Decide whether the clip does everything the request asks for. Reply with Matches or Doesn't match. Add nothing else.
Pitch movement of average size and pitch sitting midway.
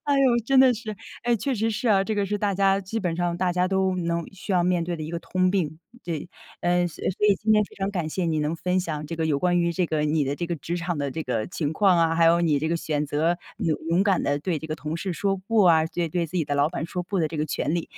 Matches